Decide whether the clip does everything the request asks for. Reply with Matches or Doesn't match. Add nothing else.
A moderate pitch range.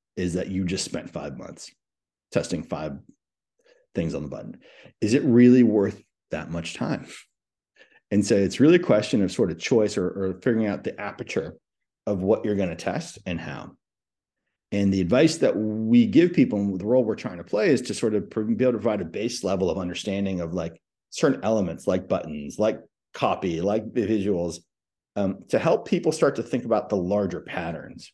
Matches